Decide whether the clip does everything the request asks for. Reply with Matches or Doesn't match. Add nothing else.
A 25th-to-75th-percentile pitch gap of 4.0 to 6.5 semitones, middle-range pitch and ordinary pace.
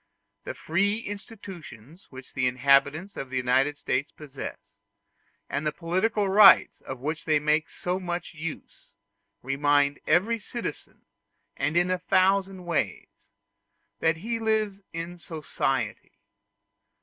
Doesn't match